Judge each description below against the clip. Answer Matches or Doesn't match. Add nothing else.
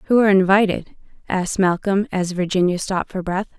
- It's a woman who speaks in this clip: Matches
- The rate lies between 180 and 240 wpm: Doesn't match